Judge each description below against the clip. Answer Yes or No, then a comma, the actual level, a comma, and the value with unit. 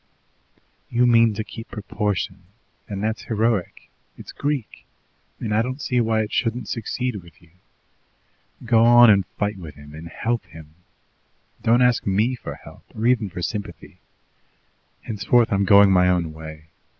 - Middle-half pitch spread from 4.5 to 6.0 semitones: No, average, 4.1 semitones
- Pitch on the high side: No, low, 110 Hz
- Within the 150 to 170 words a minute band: Yes, average, 155 wpm